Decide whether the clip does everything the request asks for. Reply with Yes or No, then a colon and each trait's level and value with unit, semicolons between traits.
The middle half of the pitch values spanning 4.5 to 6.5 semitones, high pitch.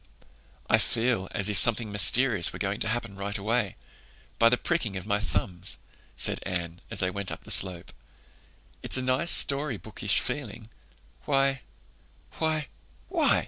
No: average, 4.8 semitones; low, 105 Hz